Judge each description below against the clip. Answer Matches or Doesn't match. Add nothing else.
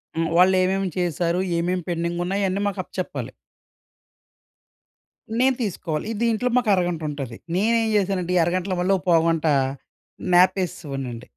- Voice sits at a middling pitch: Matches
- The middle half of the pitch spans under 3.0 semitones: Matches